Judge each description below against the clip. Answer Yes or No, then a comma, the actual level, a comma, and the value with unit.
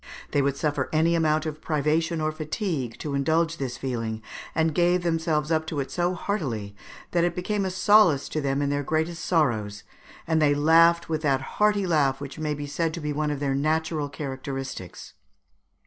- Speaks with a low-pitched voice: No, medium, 155 Hz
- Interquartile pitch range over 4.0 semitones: No, average, 3.0 semitones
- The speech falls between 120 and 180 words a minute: No, average, 195 wpm